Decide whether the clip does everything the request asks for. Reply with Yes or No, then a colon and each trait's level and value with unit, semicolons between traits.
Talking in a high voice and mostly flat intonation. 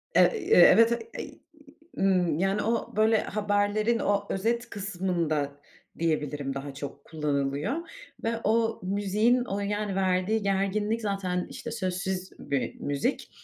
No: high, 195 Hz; average, 4.4 semitones